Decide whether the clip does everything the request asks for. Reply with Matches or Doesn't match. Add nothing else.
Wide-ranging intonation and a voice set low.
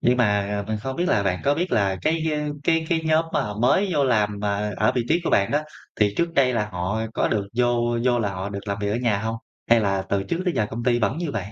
Matches